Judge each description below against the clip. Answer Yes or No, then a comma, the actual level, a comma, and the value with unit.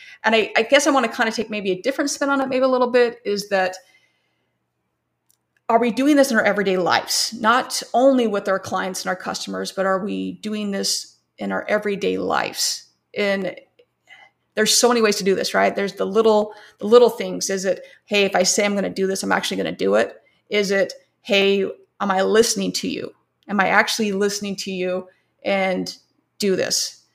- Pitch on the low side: No, high, 205 Hz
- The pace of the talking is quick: Yes, fast, 210 wpm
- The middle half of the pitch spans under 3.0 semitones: No, average, 3.7 semitones